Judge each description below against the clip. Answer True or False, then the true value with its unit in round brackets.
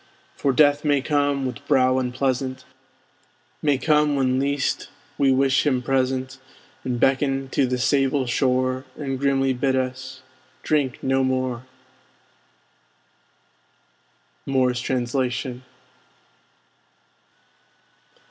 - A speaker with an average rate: False (100 wpm)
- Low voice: True (130 Hz)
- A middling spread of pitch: False (1.3 semitones)